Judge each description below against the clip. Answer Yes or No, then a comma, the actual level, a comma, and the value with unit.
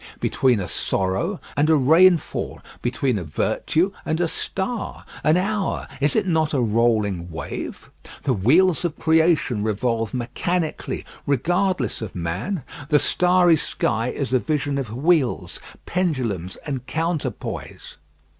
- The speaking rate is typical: No, slow, 130 wpm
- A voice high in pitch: No, medium, 140 Hz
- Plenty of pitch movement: Yes, wide, 6.9 semitones